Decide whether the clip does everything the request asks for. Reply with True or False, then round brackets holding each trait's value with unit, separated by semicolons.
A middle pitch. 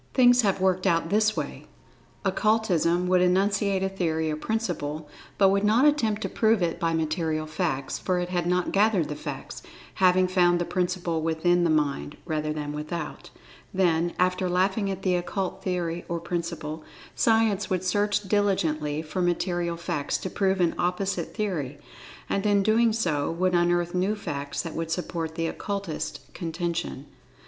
True (180 Hz)